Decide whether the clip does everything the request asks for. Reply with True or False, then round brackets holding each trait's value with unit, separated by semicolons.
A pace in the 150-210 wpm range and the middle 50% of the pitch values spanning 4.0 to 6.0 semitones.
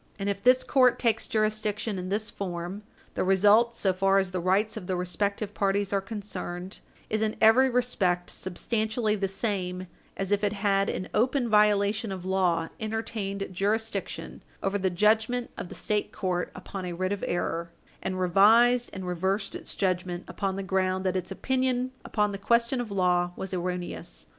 False (175 wpm; 2.8 semitones)